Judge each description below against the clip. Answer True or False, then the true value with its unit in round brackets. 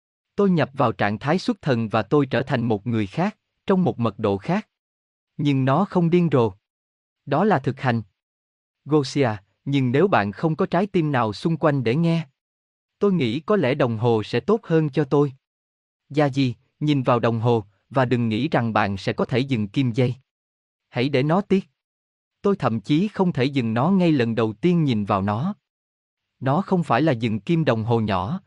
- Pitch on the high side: False (130 Hz)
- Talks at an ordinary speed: True (200 wpm)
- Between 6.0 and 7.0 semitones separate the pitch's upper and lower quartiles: True (6.4 semitones)